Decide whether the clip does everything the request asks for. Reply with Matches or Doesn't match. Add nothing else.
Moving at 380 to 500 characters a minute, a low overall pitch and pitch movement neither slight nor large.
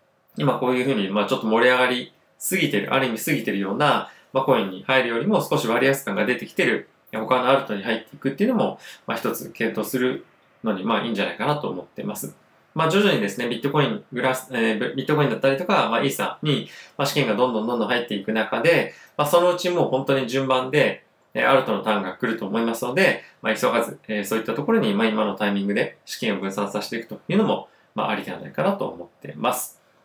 Matches